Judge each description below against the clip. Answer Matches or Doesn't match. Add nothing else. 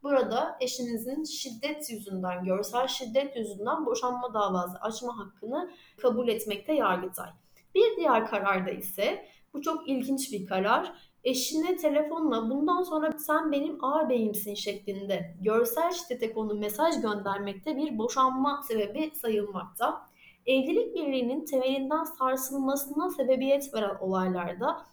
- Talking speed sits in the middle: Matches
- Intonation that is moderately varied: Doesn't match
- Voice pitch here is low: Doesn't match